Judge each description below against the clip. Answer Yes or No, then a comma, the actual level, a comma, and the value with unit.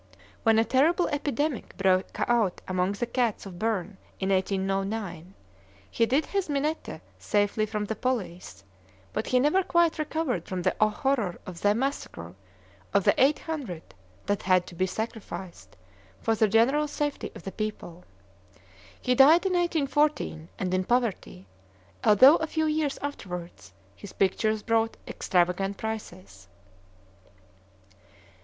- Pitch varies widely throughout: Yes, wide, 6.9 semitones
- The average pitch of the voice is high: Yes, high, 220 Hz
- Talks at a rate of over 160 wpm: No, slow, 135 wpm